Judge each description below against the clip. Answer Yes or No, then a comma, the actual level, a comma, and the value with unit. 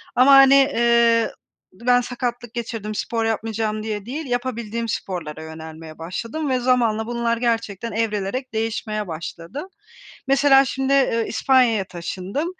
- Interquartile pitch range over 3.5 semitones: No, average, 3.2 semitones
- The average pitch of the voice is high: Yes, high, 230 Hz